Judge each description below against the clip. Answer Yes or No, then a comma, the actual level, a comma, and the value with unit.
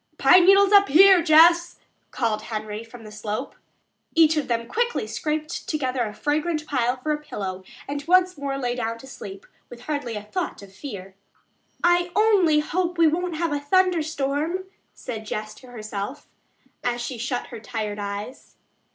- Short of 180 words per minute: Yes, average, 170 wpm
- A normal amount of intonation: No, wide, 6.9 semitones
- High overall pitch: Yes, very high, 280 Hz